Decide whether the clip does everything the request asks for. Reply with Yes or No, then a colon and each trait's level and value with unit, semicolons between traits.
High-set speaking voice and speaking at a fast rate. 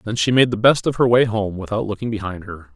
No: low, 110 Hz; fast, 285 wpm